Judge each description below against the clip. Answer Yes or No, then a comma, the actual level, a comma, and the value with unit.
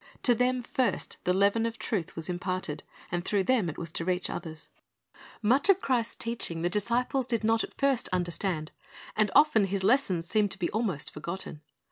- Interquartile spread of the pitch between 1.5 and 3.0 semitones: No, average, 5.2 semitones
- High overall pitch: Yes, high, 200 Hz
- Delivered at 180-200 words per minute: Yes, average, 185 wpm